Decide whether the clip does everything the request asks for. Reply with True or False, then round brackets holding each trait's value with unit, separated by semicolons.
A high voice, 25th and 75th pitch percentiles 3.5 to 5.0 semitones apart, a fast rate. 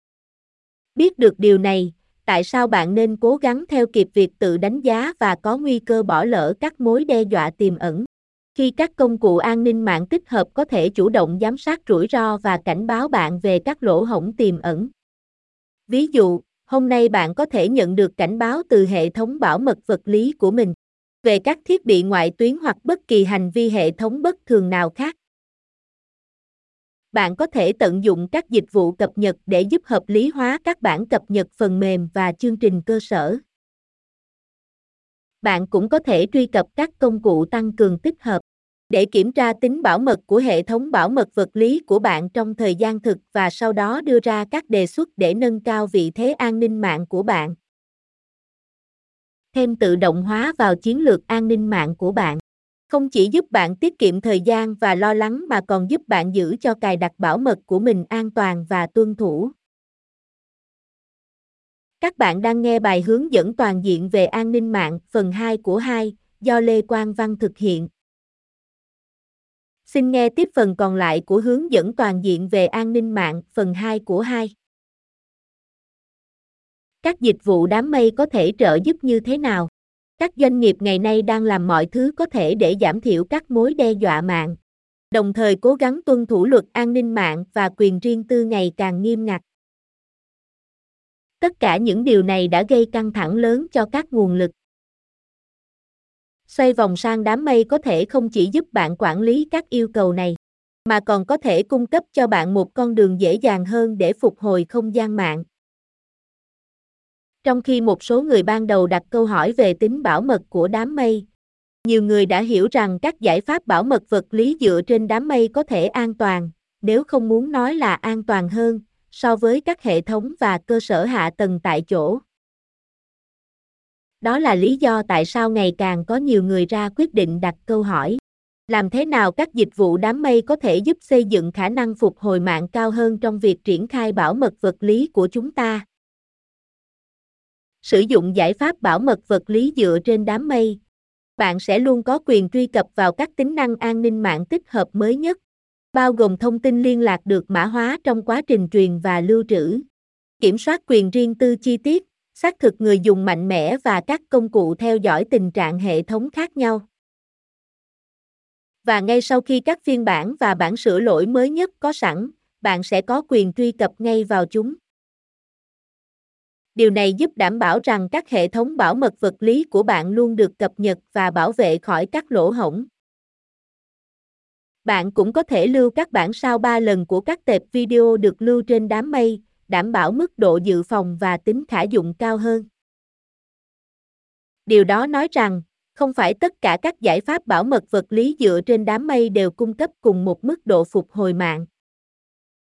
False (220 Hz; 4.3 semitones; 200 wpm)